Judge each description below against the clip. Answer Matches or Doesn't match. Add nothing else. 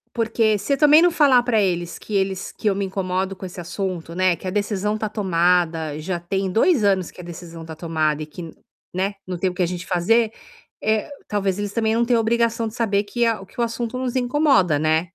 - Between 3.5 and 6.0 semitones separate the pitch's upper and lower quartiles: Matches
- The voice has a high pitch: Matches